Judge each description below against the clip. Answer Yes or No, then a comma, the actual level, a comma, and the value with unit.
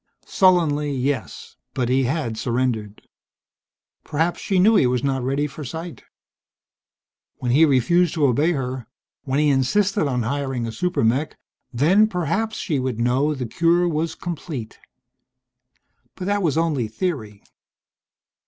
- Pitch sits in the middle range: Yes, medium, 145 Hz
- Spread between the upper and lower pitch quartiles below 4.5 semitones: No, average, 5.2 semitones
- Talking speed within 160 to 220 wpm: No, average, 140 wpm